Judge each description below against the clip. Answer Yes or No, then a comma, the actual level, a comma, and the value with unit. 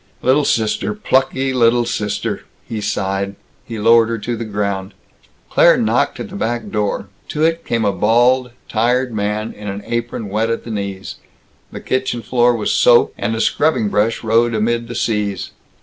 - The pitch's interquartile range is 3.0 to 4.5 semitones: No, narrow, 2.4 semitones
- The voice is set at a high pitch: No, low, 115 Hz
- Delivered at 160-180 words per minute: Yes, average, 175 wpm